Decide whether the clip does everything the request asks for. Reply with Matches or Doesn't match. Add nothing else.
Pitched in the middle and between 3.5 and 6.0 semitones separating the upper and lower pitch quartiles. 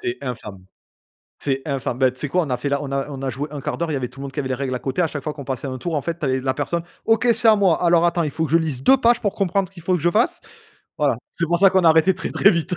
Matches